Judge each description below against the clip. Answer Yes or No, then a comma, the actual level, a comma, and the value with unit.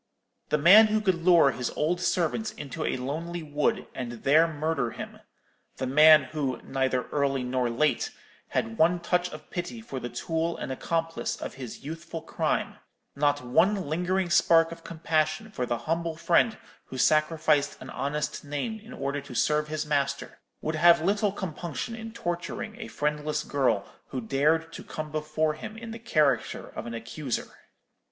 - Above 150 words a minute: Yes, average, 160 wpm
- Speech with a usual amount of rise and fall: Yes, average, 3.7 semitones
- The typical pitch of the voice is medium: Yes, medium, 155 Hz